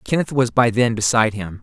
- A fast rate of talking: Yes, fast, 220 wpm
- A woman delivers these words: No, male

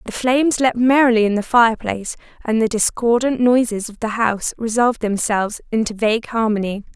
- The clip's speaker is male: No, female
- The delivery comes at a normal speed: Yes, average, 165 wpm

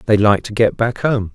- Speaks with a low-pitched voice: Yes, low, 110 Hz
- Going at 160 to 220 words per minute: No, fast, 265 wpm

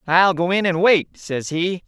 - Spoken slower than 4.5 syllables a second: Yes, 4.2 syllables/s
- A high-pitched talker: No, medium, 175 Hz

